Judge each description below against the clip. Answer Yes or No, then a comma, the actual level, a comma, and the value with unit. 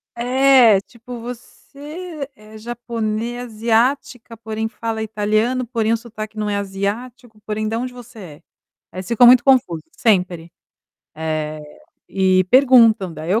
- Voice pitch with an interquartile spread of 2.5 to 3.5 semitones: Yes, average, 3.0 semitones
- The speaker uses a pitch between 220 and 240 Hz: Yes, high, 225 Hz